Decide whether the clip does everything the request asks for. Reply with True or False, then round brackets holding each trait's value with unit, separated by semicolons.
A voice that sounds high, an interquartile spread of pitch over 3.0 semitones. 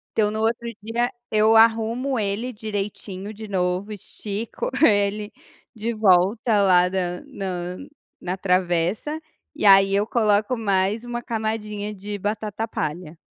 False (210 Hz; 2.6 semitones)